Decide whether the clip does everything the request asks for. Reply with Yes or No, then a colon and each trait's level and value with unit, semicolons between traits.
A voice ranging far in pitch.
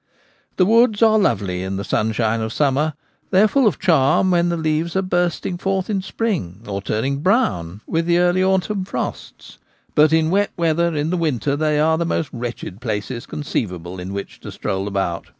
Yes: wide, 9.0 semitones